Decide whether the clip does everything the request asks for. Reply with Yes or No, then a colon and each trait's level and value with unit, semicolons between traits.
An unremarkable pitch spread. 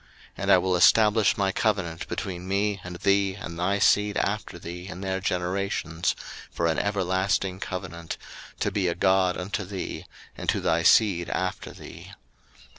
No: narrow, 2.0 semitones